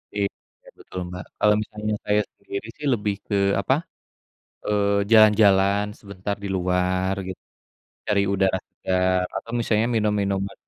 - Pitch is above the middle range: No, low, 100 Hz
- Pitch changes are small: Yes, narrow, 2.0 semitones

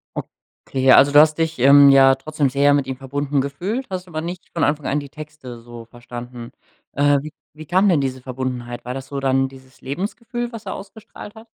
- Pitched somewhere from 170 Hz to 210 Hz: No, medium, 140 Hz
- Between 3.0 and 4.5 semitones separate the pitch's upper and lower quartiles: Yes, average, 3.3 semitones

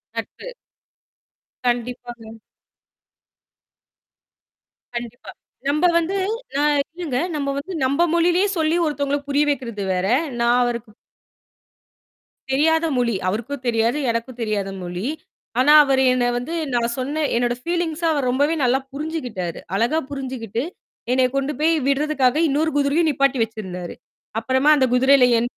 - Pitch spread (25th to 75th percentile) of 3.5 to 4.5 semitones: Yes, average, 3.9 semitones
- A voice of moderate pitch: No, very high, 260 Hz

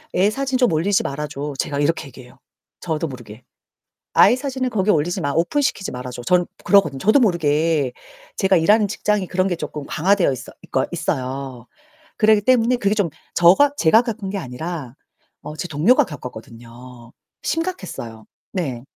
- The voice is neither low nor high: Yes, medium, 170 Hz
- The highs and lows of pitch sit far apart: Yes, wide, 7.2 semitones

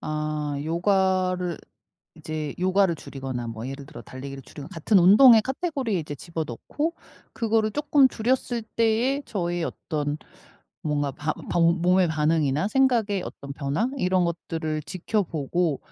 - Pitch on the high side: No, medium, 175 Hz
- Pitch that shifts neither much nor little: No, wide, 6.3 semitones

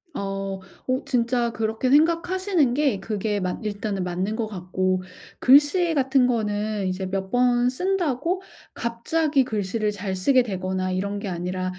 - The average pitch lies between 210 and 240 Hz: Yes, high, 220 Hz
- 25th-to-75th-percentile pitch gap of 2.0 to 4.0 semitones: No, average, 5.3 semitones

